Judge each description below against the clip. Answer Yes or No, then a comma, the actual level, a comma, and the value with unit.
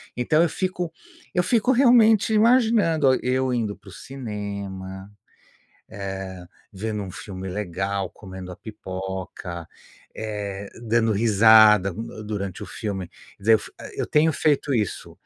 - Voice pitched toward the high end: No, low, 105 Hz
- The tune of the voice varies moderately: No, wide, 6.5 semitones